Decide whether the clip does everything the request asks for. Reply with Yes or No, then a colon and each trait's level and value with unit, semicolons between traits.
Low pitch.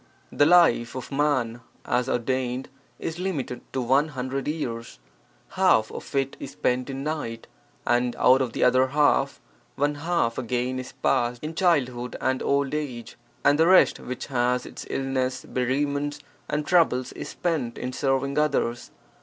Yes: low, 130 Hz